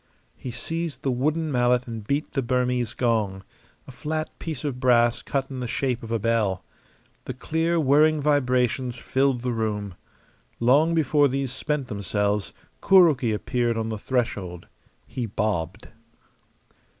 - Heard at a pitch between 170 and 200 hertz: No, low, 125 Hz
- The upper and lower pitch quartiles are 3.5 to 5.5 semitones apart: Yes, average, 3.9 semitones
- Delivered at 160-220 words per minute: No, average, 145 wpm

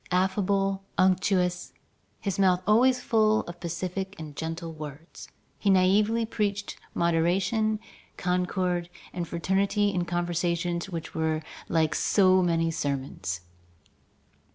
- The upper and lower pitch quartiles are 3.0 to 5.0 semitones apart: No, narrow, 2.6 semitones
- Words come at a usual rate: No, slow, 105 wpm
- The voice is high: No, medium, 180 Hz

